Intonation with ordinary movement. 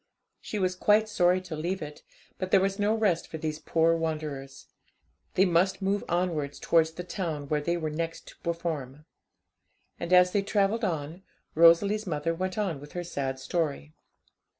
Yes: average, 3.5 semitones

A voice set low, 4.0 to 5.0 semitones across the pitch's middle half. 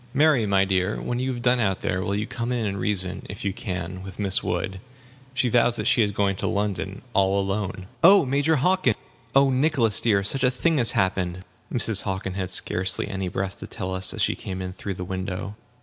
Yes: low, 100 Hz; average, 4.4 semitones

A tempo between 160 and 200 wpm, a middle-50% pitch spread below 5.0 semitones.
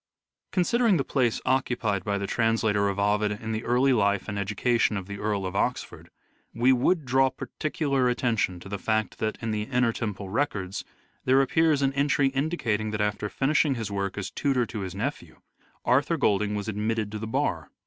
Yes: average, 190 wpm; average, 4.4 semitones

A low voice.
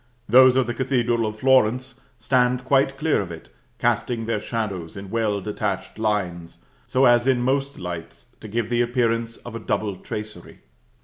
Yes: low, 115 Hz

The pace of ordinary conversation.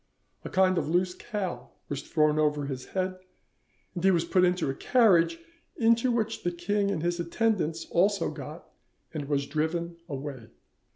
Yes: average, 165 wpm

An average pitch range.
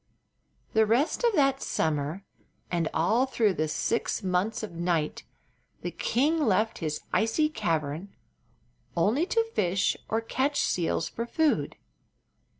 No: wide, 8.0 semitones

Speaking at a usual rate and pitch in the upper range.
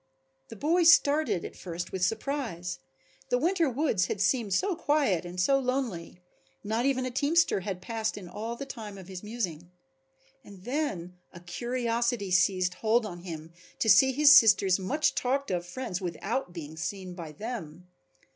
Yes: average, 165 wpm; high, 210 Hz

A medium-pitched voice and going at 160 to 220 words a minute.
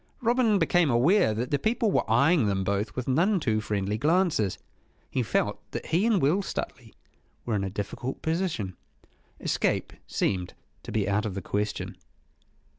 No: low, 125 Hz; average, 165 wpm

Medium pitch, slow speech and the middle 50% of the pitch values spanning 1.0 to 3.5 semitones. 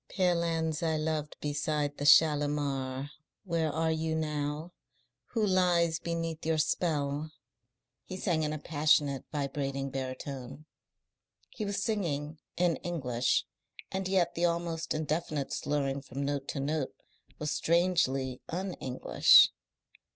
Yes: medium, 155 Hz; slow, 125 wpm; average, 2.9 semitones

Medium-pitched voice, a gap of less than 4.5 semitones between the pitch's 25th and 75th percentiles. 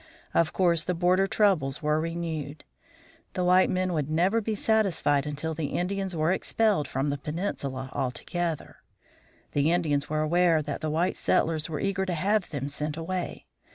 Yes: medium, 165 Hz; average, 3.6 semitones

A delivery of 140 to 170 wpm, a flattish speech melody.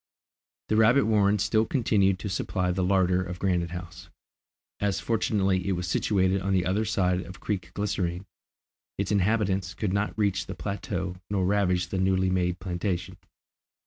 Yes: average, 160 wpm; narrow, 2.1 semitones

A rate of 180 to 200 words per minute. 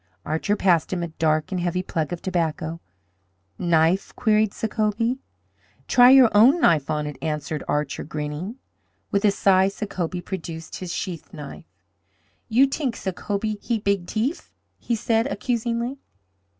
No: average, 140 wpm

